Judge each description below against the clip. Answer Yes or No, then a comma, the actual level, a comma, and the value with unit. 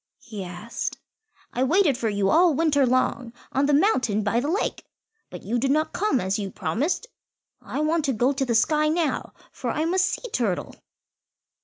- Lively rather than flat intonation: Yes, wide, 5.7 semitones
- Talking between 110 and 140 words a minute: No, average, 185 wpm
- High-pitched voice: Yes, very high, 270 Hz